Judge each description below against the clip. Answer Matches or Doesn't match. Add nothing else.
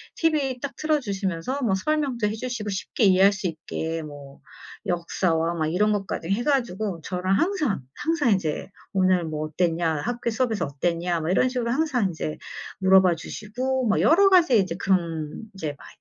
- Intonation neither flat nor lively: Doesn't match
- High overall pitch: Matches